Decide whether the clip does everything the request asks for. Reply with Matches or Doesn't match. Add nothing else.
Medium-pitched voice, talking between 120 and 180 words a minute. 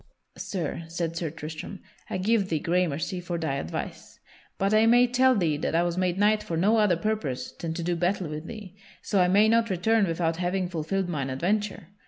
Doesn't match